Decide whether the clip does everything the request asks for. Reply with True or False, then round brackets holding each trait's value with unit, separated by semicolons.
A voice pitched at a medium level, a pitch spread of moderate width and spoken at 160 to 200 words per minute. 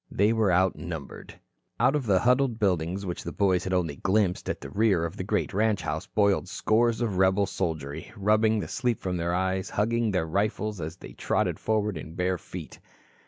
False (95 Hz; 3.3 semitones; 195 wpm)